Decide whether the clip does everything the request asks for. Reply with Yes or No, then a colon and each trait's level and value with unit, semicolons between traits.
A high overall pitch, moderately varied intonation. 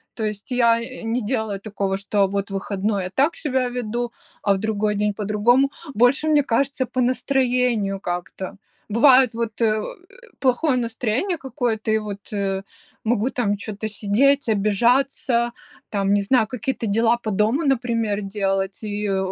Yes: high, 220 Hz; average, 3.6 semitones